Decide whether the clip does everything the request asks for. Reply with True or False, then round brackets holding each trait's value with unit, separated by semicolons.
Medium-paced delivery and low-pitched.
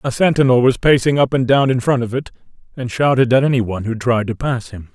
False (255 wpm; 125 Hz)